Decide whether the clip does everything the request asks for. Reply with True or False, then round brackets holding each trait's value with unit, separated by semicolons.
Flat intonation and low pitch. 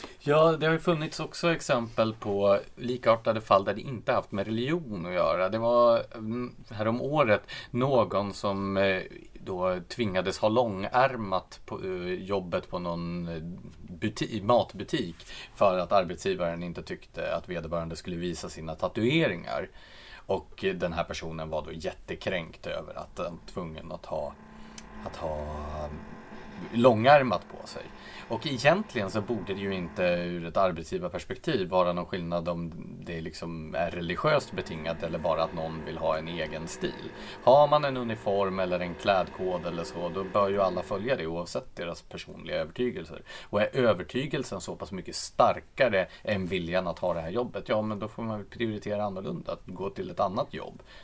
False (5.3 semitones; 100 Hz)